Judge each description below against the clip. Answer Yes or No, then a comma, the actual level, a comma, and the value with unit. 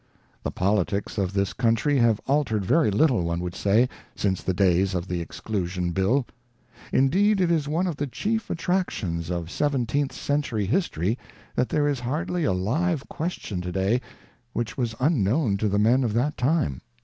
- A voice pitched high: No, low, 115 Hz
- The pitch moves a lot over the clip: Yes, wide, 7.3 semitones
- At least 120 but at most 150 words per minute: No, average, 175 wpm